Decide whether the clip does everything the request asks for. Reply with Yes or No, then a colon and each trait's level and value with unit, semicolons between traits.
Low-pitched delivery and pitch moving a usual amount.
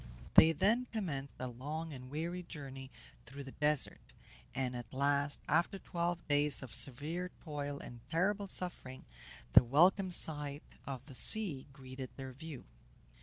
No: medium, 145 Hz; average, 4.2 semitones